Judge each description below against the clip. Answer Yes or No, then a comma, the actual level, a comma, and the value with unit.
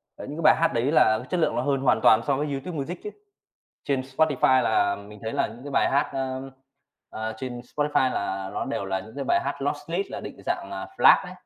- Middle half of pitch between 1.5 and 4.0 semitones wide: No, average, 4.7 semitones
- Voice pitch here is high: No, low, 130 Hz